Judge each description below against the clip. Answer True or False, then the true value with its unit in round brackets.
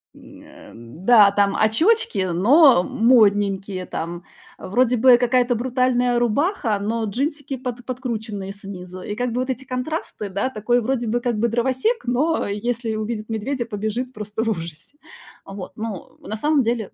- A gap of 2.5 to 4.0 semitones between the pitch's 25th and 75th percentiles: True (3.7 semitones)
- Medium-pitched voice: False (230 Hz)